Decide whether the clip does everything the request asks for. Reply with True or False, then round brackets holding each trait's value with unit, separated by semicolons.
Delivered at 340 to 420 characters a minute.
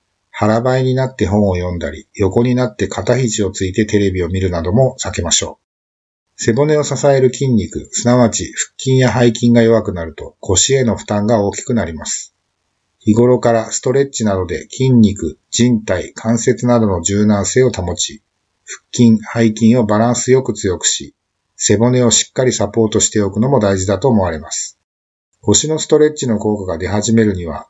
True (345 characters per minute)